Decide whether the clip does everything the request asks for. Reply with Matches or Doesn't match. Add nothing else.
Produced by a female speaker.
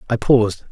Doesn't match